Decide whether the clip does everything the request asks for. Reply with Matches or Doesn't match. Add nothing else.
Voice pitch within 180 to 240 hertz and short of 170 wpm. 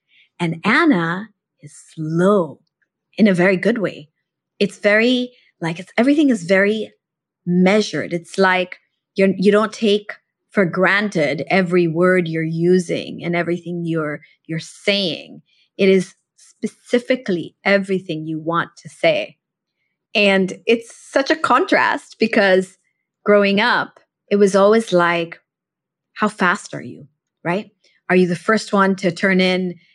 Matches